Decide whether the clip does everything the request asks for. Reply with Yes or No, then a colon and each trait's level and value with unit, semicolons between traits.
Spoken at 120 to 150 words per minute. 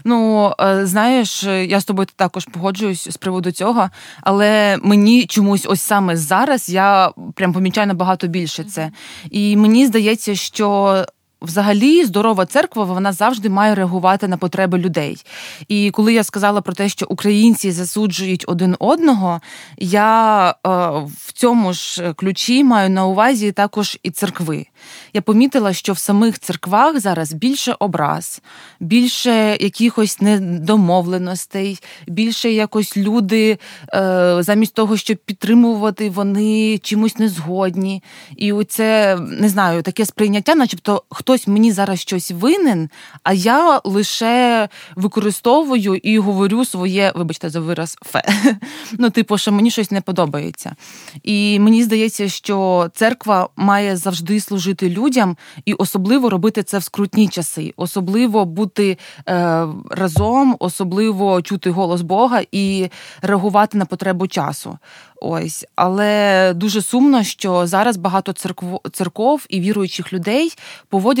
Yes: average, 130 wpm